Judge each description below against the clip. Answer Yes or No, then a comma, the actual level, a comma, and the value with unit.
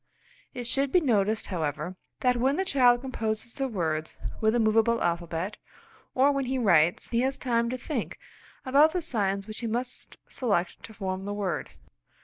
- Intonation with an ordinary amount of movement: Yes, average, 4.9 semitones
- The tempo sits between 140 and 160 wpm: No, average, 175 wpm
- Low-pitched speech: No, high, 230 Hz